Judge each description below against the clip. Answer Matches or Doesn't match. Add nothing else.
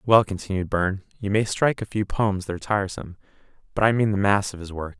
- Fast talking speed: Matches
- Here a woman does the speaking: Doesn't match